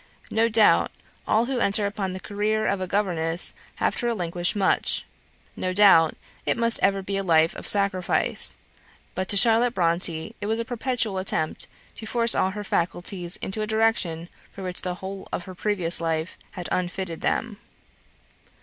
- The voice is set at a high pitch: Yes, high, 195 Hz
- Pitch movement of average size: Yes, average, 3.5 semitones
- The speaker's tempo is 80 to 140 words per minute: No, average, 170 wpm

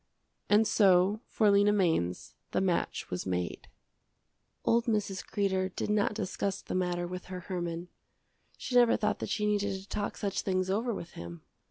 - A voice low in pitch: No, high, 195 Hz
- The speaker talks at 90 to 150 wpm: No, average, 170 wpm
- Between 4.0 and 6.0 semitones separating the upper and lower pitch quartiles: No, average, 2.8 semitones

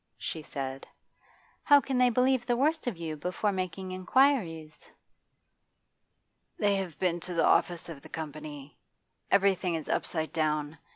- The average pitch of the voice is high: No, medium, 180 Hz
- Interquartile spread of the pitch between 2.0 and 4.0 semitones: No, wide, 5.4 semitones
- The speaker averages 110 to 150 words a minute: Yes, average, 140 wpm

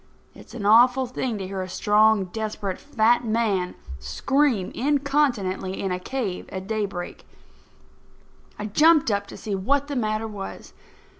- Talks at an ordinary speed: Yes, average, 145 wpm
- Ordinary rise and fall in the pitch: Yes, average, 4.7 semitones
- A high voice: Yes, high, 215 Hz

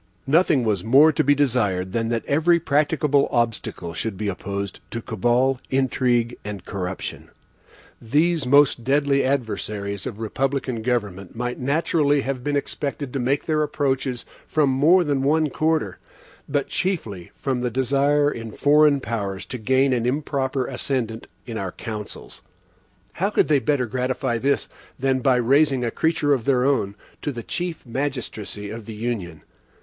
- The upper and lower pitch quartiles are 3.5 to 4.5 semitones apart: Yes, average, 4.1 semitones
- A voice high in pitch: No, low, 130 Hz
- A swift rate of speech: No, average, 155 wpm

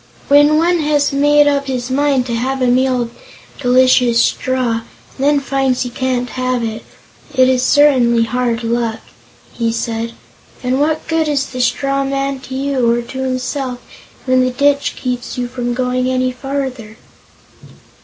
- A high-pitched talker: Yes, very high, 255 Hz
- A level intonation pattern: Yes, narrow, 2.1 semitones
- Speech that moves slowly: No, average, 165 wpm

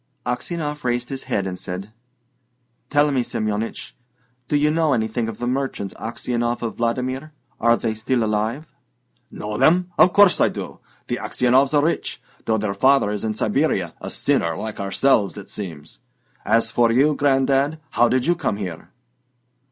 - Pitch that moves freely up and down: No, average, 4.6 semitones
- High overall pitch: No, low, 120 Hz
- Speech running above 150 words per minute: Yes, average, 165 wpm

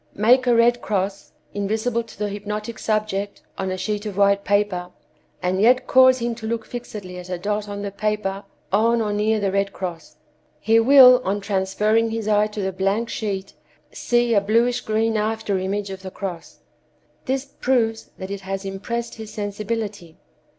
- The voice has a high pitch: Yes, high, 210 Hz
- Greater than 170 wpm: Yes, average, 180 wpm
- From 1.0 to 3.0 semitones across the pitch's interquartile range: Yes, narrow, 2.5 semitones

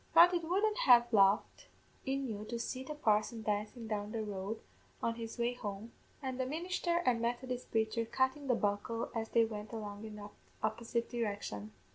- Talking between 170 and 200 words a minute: Yes, average, 185 wpm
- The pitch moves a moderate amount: Yes, average, 3.5 semitones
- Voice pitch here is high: Yes, high, 230 Hz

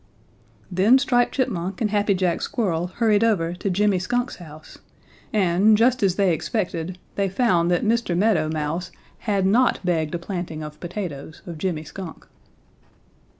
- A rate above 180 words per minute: No, average, 150 wpm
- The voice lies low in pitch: No, medium, 185 Hz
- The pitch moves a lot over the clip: No, average, 3.9 semitones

